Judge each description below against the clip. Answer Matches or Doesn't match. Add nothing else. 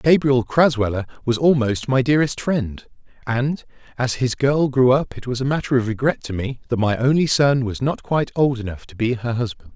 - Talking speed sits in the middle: Doesn't match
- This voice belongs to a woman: Doesn't match